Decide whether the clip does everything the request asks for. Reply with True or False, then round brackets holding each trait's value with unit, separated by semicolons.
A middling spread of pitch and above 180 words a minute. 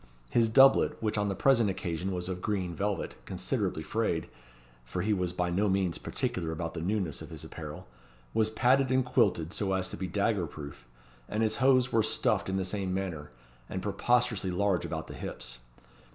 True (3.7 semitones; 190 wpm)